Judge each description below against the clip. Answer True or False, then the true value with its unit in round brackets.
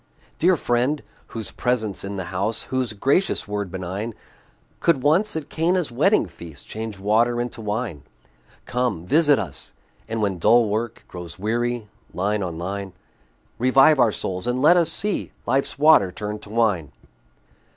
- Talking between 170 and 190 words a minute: False (150 wpm)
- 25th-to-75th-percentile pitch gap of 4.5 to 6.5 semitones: True (4.8 semitones)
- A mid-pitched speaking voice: False (115 Hz)